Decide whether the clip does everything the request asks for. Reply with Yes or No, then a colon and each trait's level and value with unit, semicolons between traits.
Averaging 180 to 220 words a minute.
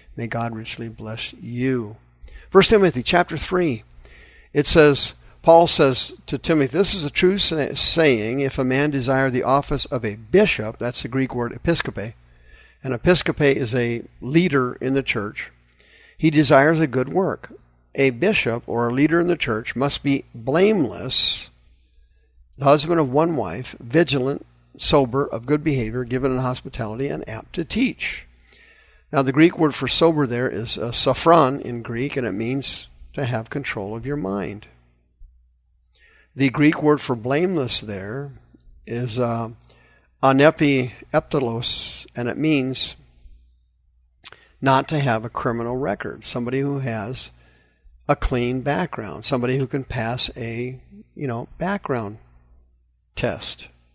No: average, 145 wpm